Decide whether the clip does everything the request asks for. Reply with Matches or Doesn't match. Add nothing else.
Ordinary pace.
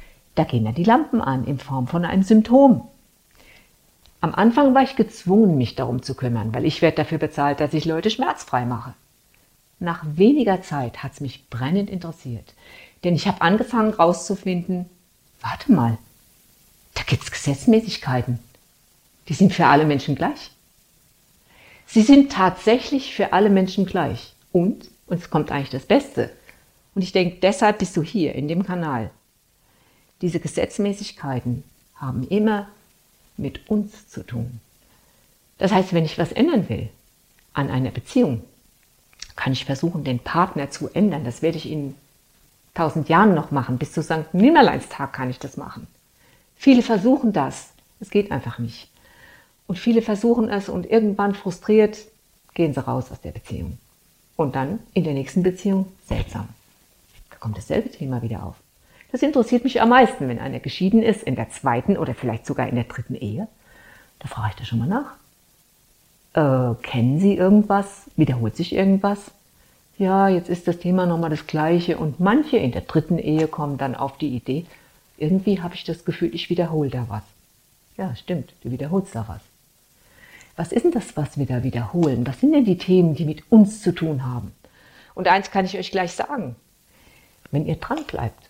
Matches